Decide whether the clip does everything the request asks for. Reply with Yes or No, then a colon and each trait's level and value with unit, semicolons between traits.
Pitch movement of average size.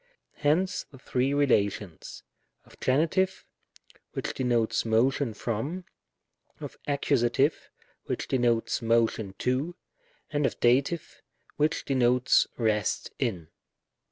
Yes: average, 3.9 semitones